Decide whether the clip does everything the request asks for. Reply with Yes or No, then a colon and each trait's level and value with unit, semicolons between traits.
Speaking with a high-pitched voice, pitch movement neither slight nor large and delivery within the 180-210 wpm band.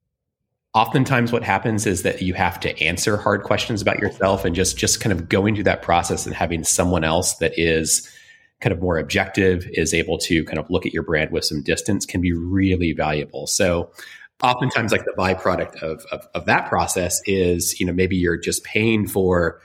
No: very low, 95 Hz; average, 3.3 semitones; average, 200 wpm